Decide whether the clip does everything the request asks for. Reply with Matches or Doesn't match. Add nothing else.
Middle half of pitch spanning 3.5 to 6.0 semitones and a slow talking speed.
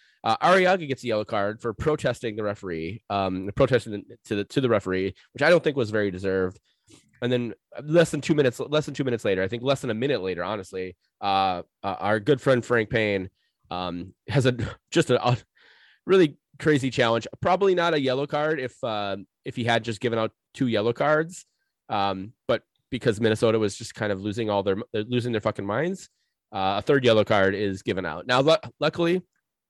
Doesn't match